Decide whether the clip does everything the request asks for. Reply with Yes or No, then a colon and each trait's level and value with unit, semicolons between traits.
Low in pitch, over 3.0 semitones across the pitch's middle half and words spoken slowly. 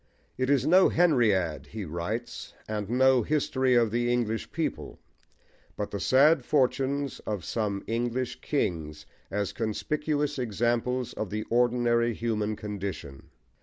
Yes: low, 120 Hz; average, 3.8 semitones; slow, 130 wpm